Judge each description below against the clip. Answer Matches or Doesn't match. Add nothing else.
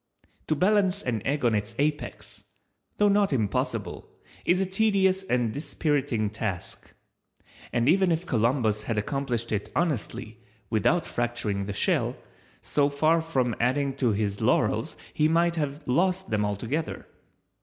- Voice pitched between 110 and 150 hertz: Matches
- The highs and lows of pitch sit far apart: Matches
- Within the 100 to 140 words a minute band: Matches